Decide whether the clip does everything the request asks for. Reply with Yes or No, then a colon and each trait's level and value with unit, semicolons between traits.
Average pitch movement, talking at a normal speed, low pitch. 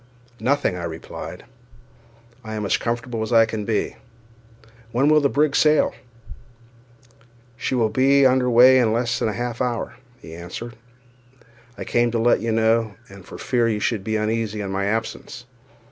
No: narrow, 2.3 semitones; average, 165 wpm; low, 115 Hz